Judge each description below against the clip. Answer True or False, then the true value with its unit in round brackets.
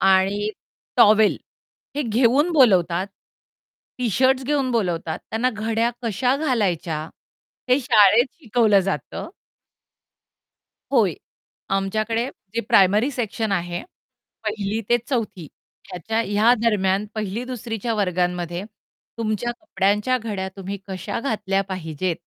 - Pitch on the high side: True (215 Hz)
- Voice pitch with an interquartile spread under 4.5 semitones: True (3.9 semitones)